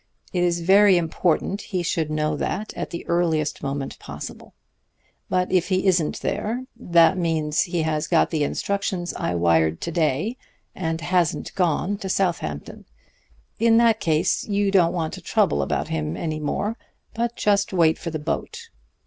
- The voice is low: No, medium, 170 Hz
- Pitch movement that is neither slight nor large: Yes, average, 3.9 semitones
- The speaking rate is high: No, average, 165 wpm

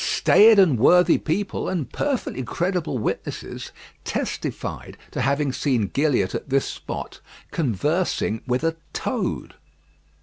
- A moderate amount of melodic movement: No, wide, 5.9 semitones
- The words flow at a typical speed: No, slow, 115 wpm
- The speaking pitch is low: No, medium, 150 Hz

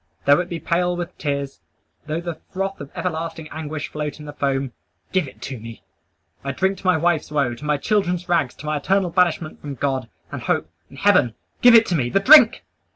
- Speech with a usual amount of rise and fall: Yes, average, 4.2 semitones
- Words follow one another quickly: Yes, fast, 215 wpm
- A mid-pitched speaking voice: Yes, medium, 155 Hz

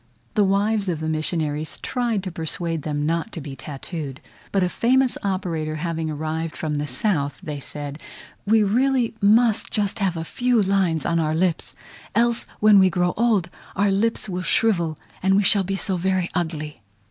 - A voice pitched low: No, medium, 180 Hz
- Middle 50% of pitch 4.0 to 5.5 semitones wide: Yes, average, 4.5 semitones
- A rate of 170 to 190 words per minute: Yes, average, 180 wpm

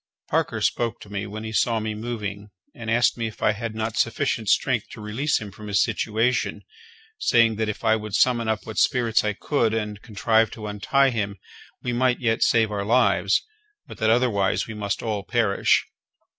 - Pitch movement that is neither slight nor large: No, narrow, 1.9 semitones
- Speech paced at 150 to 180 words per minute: No, average, 195 wpm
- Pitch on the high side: No, low, 110 Hz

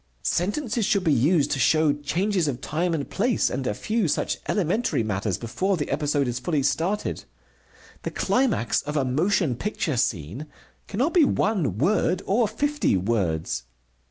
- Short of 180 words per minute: Yes, average, 155 wpm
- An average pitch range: No, wide, 8.5 semitones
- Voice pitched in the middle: Yes, medium, 155 Hz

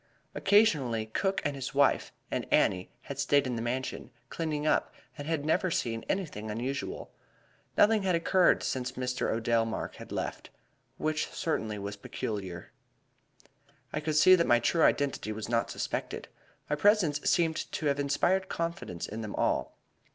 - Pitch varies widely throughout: Yes, wide, 6.4 semitones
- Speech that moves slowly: No, average, 160 wpm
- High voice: No, medium, 140 Hz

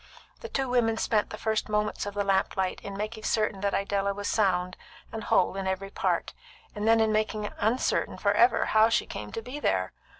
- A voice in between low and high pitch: No, high, 210 Hz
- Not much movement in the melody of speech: Yes, narrow, 2.2 semitones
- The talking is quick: Yes, fast, 210 wpm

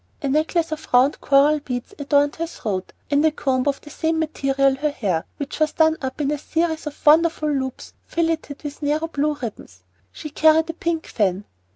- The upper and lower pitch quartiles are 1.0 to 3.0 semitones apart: Yes, average, 2.7 semitones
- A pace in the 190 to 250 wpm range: Yes, average, 195 wpm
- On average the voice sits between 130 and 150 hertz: No, very high, 295 Hz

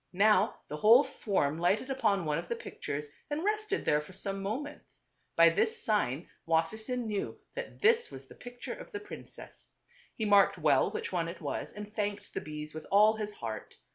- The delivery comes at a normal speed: No, fast, 210 wpm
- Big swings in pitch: Yes, wide, 6.8 semitones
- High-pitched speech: Yes, high, 205 Hz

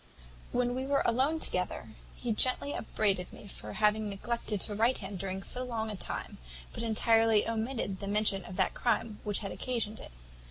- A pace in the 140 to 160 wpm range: No, average, 190 wpm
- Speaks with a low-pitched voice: No, high, 220 Hz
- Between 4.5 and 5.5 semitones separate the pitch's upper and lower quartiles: No, average, 3.0 semitones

